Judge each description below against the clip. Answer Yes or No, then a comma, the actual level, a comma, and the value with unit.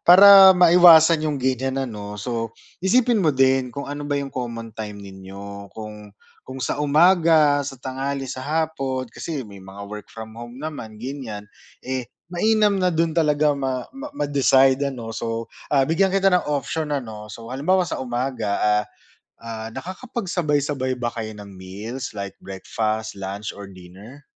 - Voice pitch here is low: Yes, low, 130 Hz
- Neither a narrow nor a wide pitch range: No, wide, 5.8 semitones